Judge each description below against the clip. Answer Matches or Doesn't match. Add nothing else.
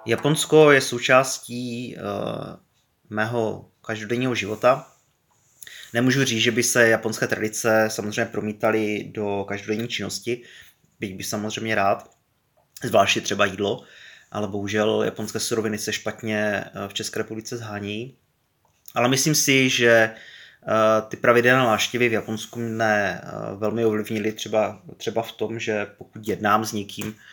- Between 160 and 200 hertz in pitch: Doesn't match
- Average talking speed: Matches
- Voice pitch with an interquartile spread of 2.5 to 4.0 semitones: Doesn't match